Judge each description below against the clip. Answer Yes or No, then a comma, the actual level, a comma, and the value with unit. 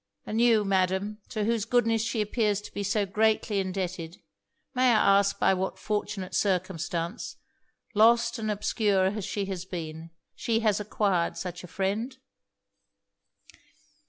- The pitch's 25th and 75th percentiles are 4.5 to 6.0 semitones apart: No, average, 2.8 semitones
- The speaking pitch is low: No, high, 205 Hz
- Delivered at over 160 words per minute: No, average, 140 wpm